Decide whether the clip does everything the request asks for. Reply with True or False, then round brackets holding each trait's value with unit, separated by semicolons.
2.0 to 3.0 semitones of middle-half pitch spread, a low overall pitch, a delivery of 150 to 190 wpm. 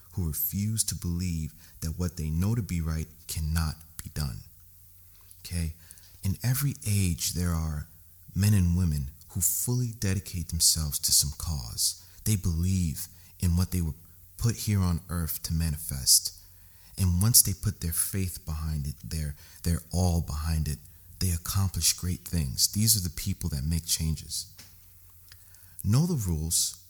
True (2.4 semitones; 90 Hz; 155 wpm)